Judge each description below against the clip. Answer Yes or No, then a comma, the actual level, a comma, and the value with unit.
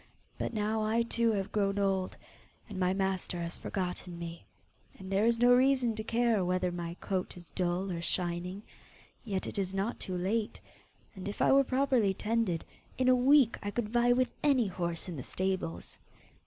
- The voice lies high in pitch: Yes, high, 195 Hz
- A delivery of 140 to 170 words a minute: No, average, 185 wpm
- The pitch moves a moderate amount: Yes, average, 4.2 semitones